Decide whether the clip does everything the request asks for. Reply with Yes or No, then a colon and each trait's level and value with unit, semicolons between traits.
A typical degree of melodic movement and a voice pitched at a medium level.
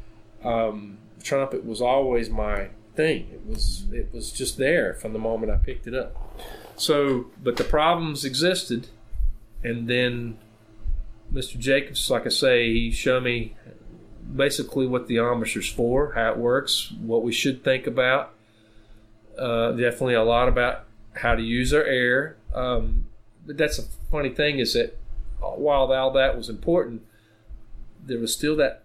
No: average, 3.2 semitones; low, 120 Hz